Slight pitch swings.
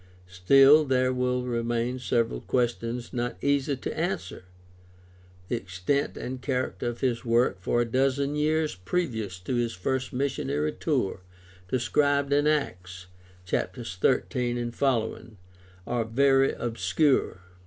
No: average, 3.0 semitones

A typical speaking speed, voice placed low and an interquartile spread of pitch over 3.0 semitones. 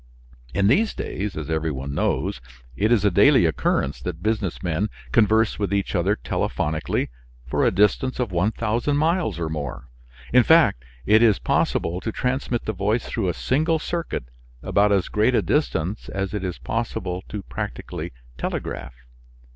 Yes: average, 165 wpm; low, 105 Hz; average, 5.1 semitones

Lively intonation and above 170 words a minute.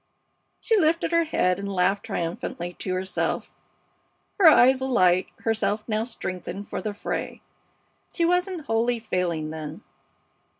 No: wide, 6.4 semitones; slow, 135 wpm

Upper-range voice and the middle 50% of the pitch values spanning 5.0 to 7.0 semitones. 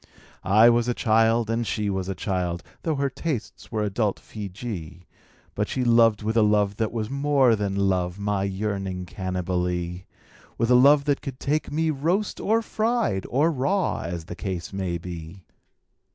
No: low, 105 Hz; wide, 5.5 semitones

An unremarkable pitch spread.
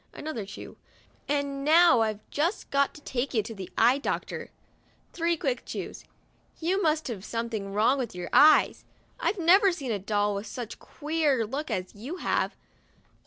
No: wide, 6.5 semitones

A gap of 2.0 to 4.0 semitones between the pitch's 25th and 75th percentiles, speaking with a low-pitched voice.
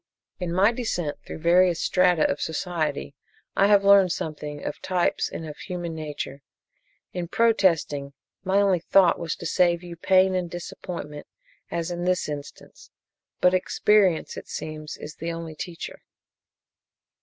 No: average, 2.8 semitones; medium, 175 Hz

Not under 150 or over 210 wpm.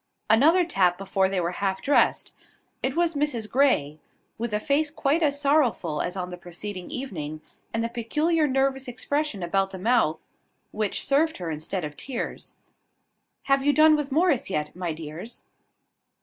Yes: average, 165 wpm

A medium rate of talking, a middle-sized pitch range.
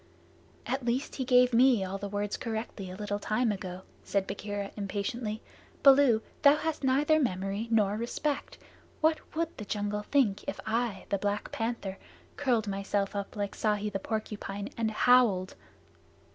Yes: average, 155 wpm; average, 3.7 semitones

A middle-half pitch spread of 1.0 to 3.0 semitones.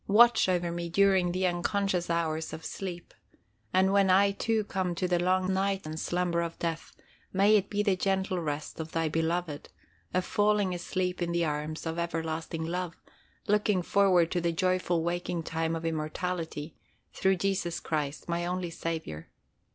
Yes: narrow, 2.5 semitones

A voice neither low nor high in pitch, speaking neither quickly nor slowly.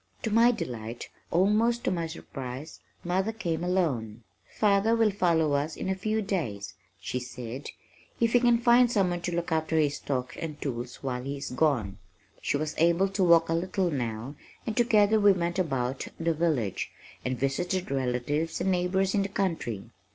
Yes: medium, 165 Hz; average, 175 wpm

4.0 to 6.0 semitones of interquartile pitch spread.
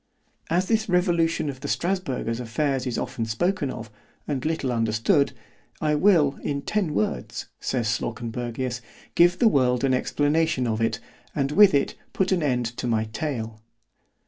Yes: wide, 5.6 semitones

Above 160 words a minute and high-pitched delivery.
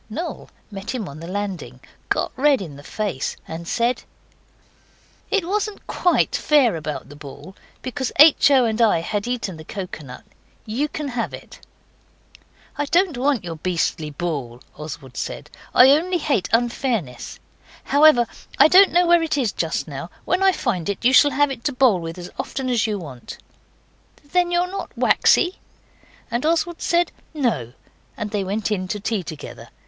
Yes: average, 170 wpm; high, 230 Hz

